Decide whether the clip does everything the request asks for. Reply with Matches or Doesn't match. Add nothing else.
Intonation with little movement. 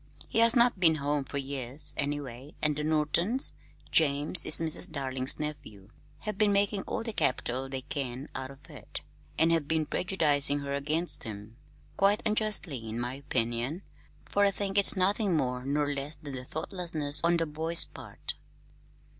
Doesn't match